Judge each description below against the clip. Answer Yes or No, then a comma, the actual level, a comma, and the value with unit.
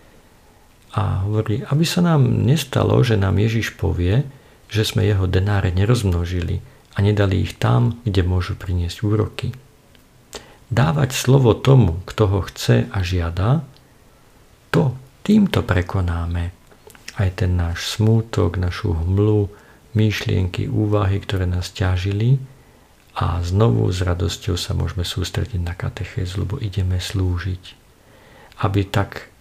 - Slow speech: No, average, 120 wpm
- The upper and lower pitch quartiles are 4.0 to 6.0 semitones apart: Yes, average, 4.3 semitones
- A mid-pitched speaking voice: No, low, 105 Hz